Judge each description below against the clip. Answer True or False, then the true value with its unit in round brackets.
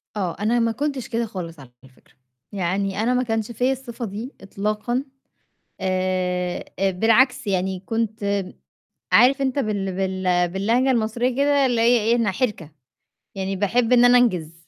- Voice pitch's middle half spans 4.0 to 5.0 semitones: True (4.4 semitones)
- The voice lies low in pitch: False (215 Hz)